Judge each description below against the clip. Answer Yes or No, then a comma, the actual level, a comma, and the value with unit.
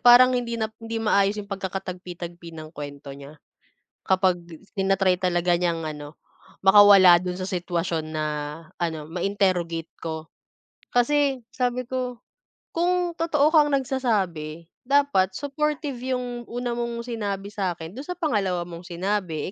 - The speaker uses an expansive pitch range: Yes, wide, 6.1 semitones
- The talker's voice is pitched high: Yes, high, 195 Hz